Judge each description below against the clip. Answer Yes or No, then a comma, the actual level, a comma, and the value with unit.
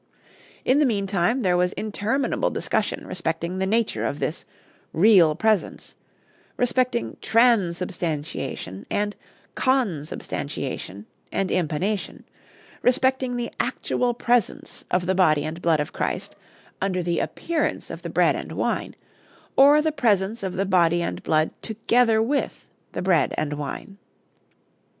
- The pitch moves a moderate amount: No, wide, 5.7 semitones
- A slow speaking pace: Yes, slow, 130 wpm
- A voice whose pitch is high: Yes, high, 195 Hz